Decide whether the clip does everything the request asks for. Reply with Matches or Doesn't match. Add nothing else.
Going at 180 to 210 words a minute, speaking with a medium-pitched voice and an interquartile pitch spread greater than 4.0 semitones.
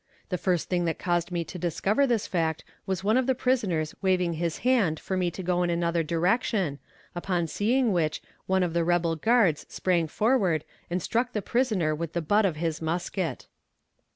Doesn't match